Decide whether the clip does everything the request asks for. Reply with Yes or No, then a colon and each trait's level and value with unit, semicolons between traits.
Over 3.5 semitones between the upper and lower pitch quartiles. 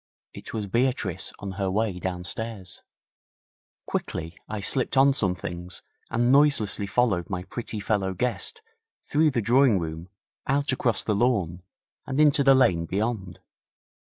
Yes: wide, 5.6 semitones